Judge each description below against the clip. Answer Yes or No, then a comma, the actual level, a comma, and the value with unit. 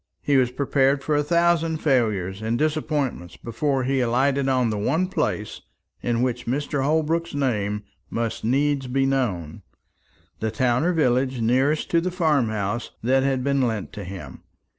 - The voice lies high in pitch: No, low, 130 Hz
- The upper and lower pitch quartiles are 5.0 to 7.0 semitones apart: No, average, 4.0 semitones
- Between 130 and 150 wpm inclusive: No, average, 160 wpm